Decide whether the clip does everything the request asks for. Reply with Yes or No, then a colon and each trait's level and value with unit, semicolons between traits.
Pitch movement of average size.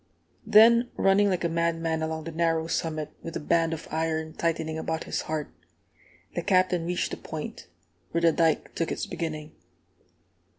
No: narrow, 1.1 semitones